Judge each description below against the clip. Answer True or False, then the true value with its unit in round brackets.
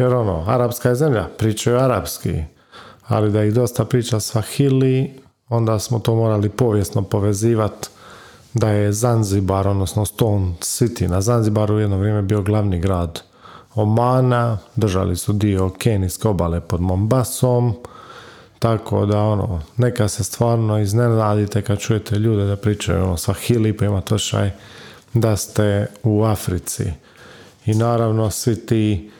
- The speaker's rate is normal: True (135 wpm)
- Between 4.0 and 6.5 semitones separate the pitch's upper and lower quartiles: False (2.6 semitones)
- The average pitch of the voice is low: True (105 Hz)